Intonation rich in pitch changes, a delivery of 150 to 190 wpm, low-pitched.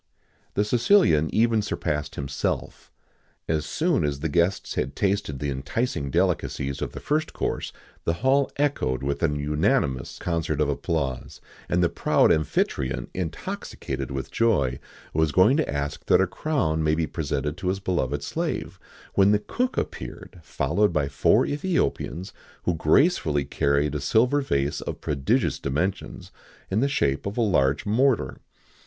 Yes: wide, 6.9 semitones; average, 155 wpm; very low, 80 Hz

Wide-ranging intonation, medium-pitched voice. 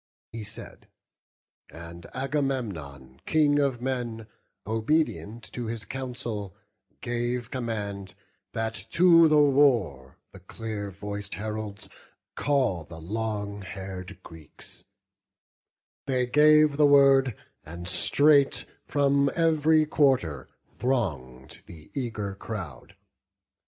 No: wide, 6.1 semitones; low, 115 Hz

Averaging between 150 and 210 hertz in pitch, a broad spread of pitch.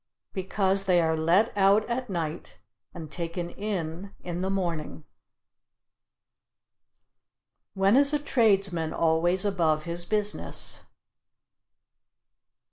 No: medium, 185 Hz; average, 3.2 semitones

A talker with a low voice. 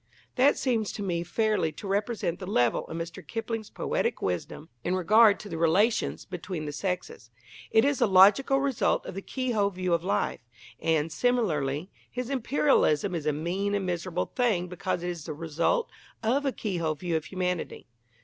No: medium, 185 Hz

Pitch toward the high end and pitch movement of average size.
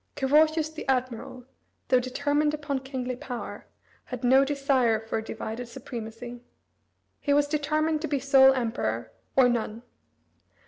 Yes: very high, 265 Hz; average, 3.1 semitones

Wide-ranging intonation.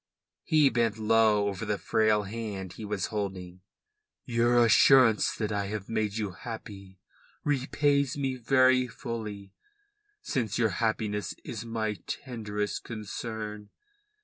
No: narrow, 2.4 semitones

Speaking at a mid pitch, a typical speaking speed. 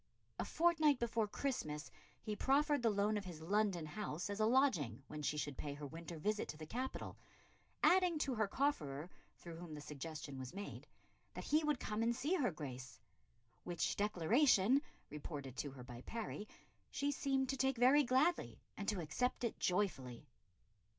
No: high, 205 Hz; average, 175 wpm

